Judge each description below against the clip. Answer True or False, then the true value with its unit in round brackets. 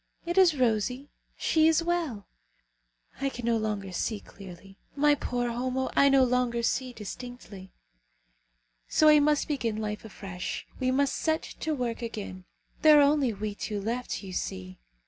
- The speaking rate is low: False (160 wpm)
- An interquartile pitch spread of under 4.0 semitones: False (5.1 semitones)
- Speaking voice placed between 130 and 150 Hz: False (245 Hz)